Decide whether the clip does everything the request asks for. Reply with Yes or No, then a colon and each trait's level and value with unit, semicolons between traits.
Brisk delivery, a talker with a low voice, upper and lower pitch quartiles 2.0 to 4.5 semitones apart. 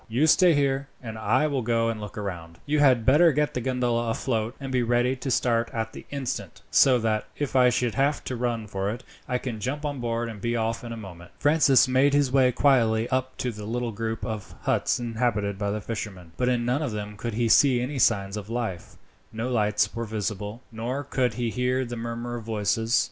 Yes: fast, 225 wpm; low, 120 Hz; average, 2.7 semitones